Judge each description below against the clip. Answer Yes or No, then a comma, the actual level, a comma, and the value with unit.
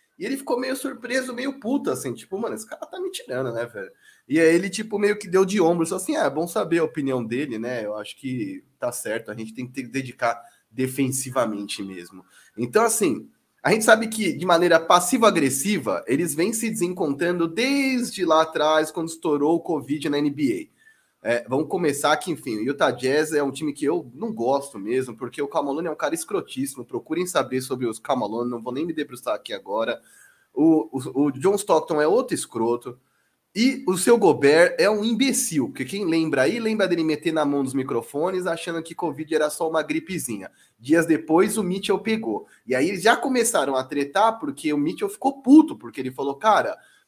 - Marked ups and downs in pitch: Yes, wide, 8.9 semitones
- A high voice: No, medium, 165 Hz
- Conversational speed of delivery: No, fast, 205 wpm